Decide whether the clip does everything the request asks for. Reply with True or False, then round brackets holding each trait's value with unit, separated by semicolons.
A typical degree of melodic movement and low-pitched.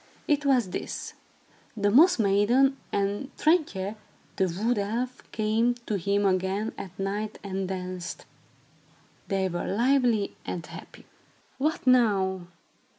False (4.4 semitones; 205 Hz)